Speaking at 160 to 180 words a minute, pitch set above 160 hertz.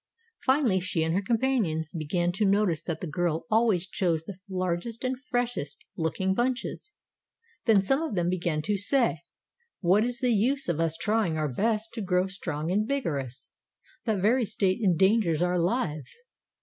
Yes: average, 165 wpm; high, 190 Hz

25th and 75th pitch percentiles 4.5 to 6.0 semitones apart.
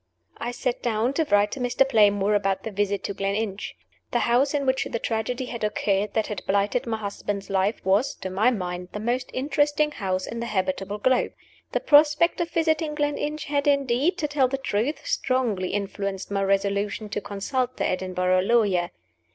Yes: average, 5.0 semitones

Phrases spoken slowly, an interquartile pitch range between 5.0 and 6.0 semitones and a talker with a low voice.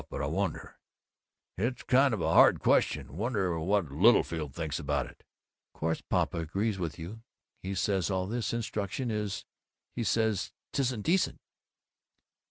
No: average, 145 wpm; wide, 5.5 semitones; low, 100 Hz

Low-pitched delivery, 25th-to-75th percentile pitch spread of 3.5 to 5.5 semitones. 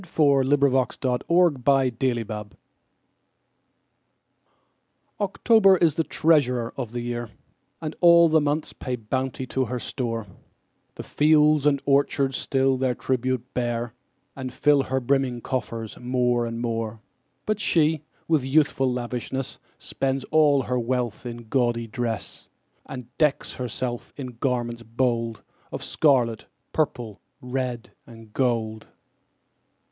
No: low, 130 Hz; average, 2.9 semitones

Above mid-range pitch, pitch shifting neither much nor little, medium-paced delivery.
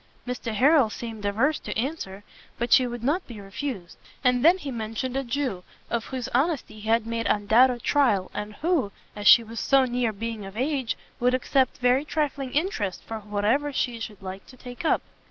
Yes: high, 240 Hz; average, 3.9 semitones; average, 190 wpm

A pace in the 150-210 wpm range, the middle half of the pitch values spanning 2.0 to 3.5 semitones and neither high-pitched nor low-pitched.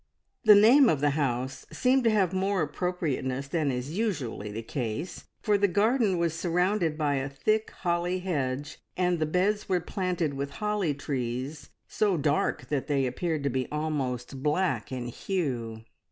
No: average, 165 wpm; wide, 5.6 semitones; medium, 155 Hz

